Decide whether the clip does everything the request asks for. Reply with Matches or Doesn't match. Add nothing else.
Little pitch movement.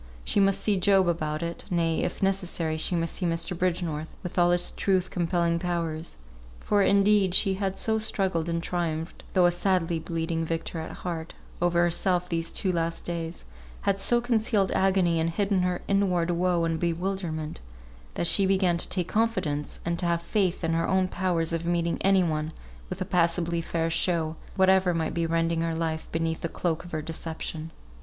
Matches